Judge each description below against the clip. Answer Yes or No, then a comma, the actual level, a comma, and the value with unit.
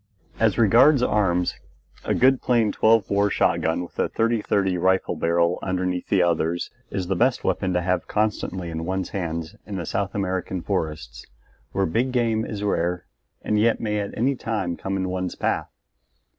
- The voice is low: Yes, very low, 95 Hz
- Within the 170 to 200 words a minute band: Yes, average, 175 wpm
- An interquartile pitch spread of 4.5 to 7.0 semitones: No, average, 3.5 semitones